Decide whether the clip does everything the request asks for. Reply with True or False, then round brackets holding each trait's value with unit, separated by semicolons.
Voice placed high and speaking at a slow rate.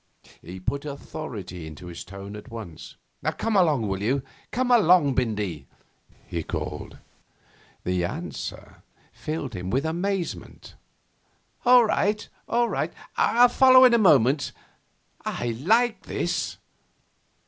False (135 Hz; 120 wpm)